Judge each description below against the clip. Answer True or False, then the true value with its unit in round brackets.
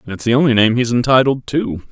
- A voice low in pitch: True (125 Hz)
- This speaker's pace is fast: True (250 wpm)